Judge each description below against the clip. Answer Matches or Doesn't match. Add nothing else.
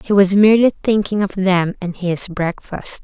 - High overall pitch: Matches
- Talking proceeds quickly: Doesn't match